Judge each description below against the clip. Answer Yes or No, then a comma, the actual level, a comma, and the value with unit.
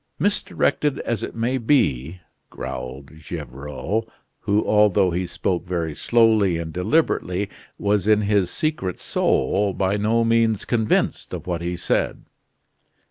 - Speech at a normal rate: No, slow, 130 wpm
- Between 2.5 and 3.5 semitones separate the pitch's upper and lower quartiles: No, average, 4.4 semitones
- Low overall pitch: Yes, low, 100 Hz